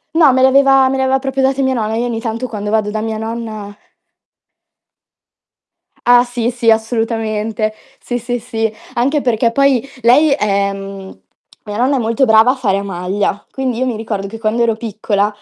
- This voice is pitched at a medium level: No, high, 230 Hz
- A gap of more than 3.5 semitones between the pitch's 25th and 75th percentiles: No, average, 3.0 semitones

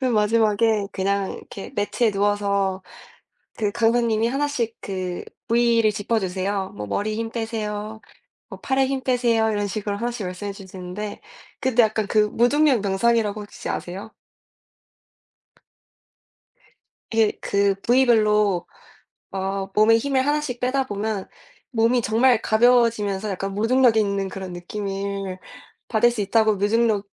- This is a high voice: Yes, high, 215 Hz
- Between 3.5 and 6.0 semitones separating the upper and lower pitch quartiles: No, average, 2.8 semitones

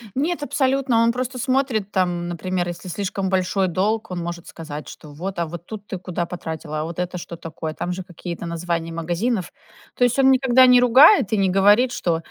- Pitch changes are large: Yes, wide, 5.9 semitones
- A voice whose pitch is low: No, medium, 185 Hz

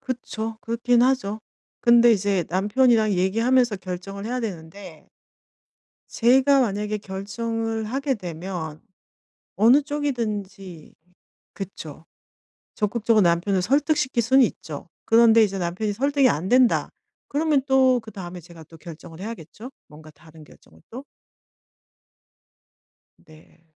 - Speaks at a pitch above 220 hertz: No, high, 215 Hz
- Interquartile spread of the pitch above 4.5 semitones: Yes, average, 5.2 semitones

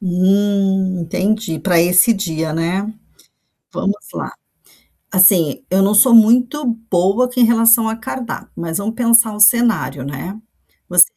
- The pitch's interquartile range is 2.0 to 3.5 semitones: No, average, 4.1 semitones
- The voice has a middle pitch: No, high, 200 Hz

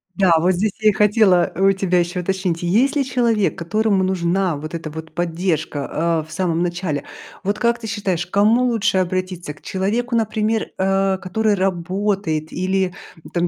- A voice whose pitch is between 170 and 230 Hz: Yes, high, 190 Hz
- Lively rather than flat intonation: No, average, 3.3 semitones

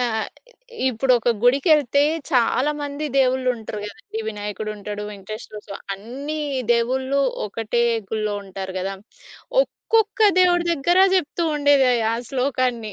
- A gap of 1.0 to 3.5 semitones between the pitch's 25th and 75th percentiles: No, average, 4.9 semitones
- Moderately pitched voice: No, very high, 250 Hz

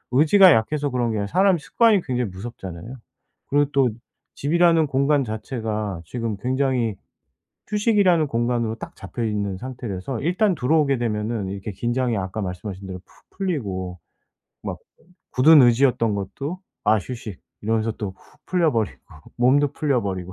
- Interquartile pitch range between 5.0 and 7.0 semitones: Yes, wide, 5.6 semitones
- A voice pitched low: Yes, low, 120 Hz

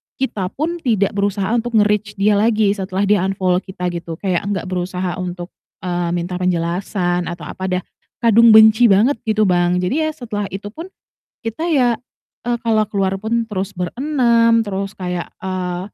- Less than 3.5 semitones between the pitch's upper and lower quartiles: No, average, 3.8 semitones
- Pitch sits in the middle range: No, high, 200 Hz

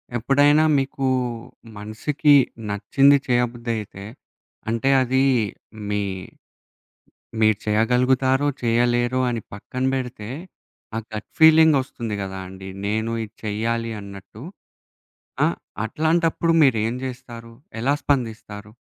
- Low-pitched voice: Yes, low, 120 Hz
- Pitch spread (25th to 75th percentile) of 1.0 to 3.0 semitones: No, average, 3.6 semitones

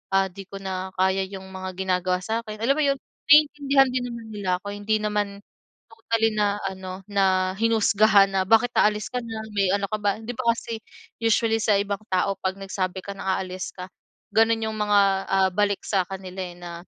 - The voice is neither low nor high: No, high, 200 Hz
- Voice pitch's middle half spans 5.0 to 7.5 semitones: No, average, 2.8 semitones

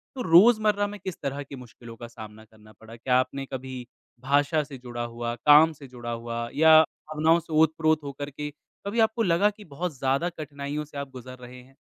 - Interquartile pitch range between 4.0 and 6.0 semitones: Yes, average, 4.4 semitones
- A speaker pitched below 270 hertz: Yes, medium, 140 Hz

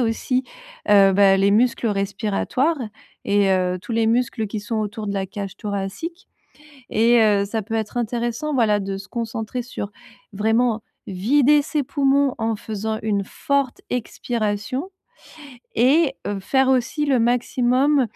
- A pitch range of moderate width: Yes, average, 3.7 semitones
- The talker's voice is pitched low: No, high, 225 Hz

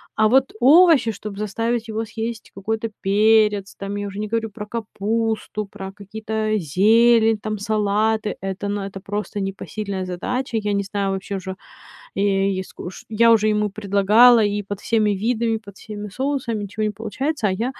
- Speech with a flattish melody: Yes, narrow, 2.0 semitones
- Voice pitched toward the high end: Yes, high, 210 Hz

